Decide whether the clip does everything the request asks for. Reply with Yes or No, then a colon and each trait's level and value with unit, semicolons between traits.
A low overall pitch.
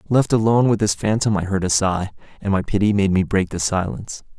Yes: low, 100 Hz